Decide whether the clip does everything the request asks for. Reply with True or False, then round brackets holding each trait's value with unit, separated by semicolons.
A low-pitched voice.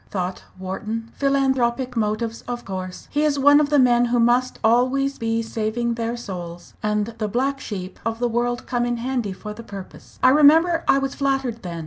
False (235 Hz)